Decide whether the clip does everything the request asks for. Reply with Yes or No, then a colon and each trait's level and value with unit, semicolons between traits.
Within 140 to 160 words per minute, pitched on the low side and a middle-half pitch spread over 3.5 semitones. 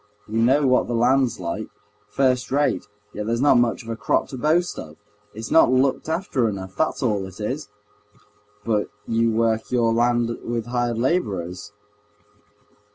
No: average, 155 wpm; low, 115 Hz; average, 3.0 semitones